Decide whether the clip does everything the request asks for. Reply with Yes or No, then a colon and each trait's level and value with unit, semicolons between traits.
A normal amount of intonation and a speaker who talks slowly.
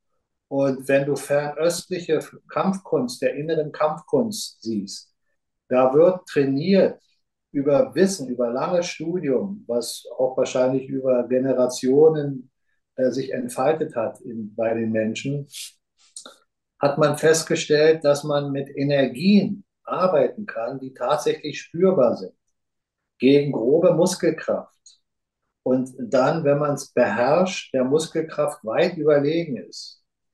Yes: average, 3.8 semitones; slow, 115 wpm